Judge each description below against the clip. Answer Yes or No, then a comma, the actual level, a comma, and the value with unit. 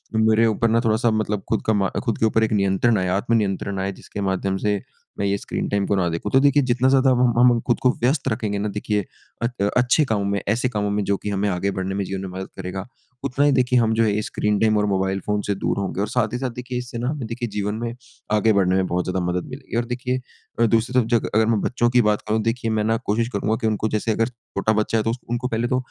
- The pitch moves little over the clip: No, average, 3.1 semitones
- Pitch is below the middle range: Yes, low, 110 Hz